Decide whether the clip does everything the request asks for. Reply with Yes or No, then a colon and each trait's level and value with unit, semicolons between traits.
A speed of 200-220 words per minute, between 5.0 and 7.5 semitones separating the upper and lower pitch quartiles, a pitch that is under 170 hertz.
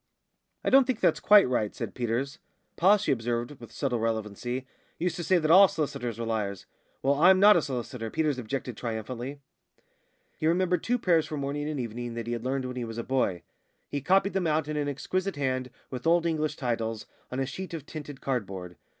Yes: fast, 205 wpm; wide, 5.5 semitones; low, 135 Hz